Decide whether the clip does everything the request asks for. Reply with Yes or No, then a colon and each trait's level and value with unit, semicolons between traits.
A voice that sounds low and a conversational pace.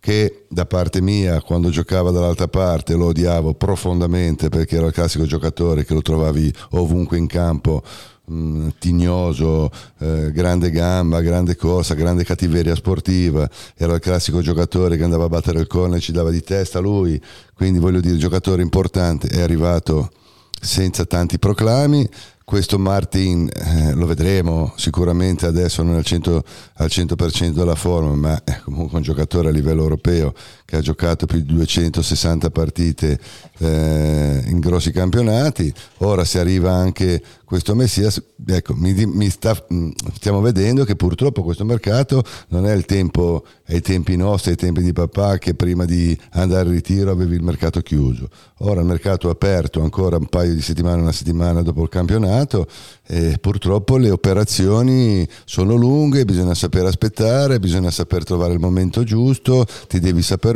Yes: very low, 90 Hz; average, 160 wpm